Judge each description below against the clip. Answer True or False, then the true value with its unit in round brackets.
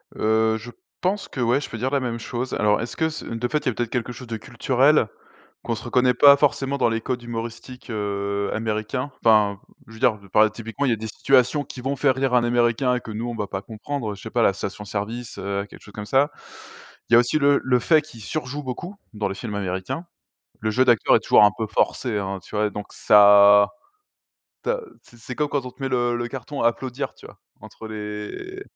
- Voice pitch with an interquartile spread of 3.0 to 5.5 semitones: True (3.5 semitones)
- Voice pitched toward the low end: True (120 Hz)